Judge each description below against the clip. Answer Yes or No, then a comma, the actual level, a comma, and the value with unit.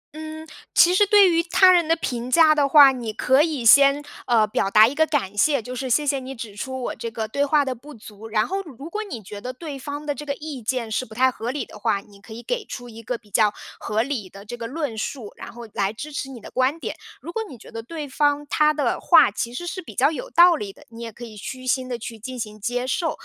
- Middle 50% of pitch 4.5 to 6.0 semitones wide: Yes, average, 5.0 semitones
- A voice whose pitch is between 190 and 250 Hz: No, very high, 260 Hz